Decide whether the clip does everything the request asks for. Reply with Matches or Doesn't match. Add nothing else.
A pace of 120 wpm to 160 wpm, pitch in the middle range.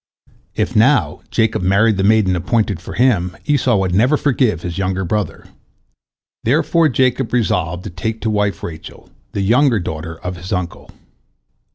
Doesn't match